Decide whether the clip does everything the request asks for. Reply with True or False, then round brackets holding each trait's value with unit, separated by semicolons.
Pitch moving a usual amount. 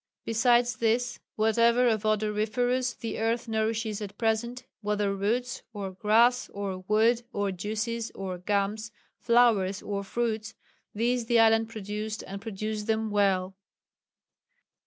False (2.2 semitones)